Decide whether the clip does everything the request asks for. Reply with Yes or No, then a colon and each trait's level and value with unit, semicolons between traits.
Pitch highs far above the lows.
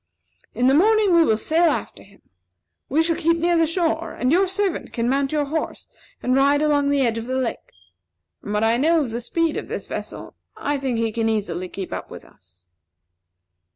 Yes: wide, 6.2 semitones